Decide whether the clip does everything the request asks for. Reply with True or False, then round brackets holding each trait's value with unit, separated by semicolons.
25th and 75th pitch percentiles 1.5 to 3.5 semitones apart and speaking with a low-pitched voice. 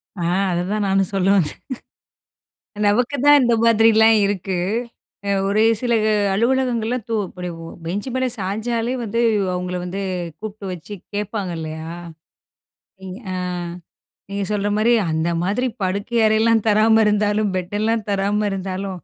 False (2.9 semitones; 205 Hz)